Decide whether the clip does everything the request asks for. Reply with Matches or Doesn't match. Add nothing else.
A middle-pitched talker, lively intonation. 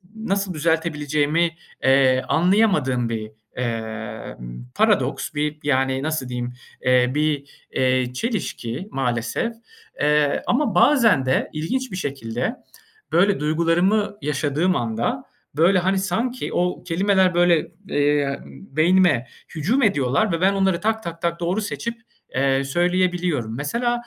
Matches